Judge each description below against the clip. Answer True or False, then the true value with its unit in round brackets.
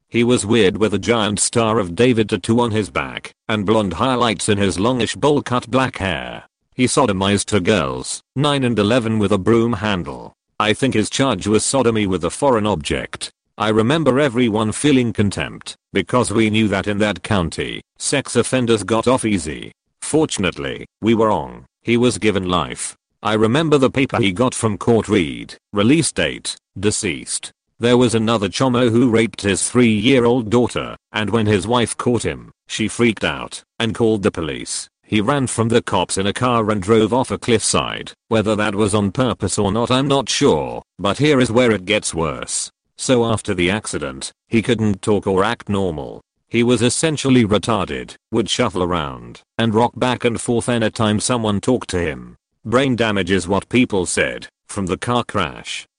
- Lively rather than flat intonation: False (3.3 semitones)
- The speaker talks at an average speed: True (185 wpm)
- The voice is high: False (110 Hz)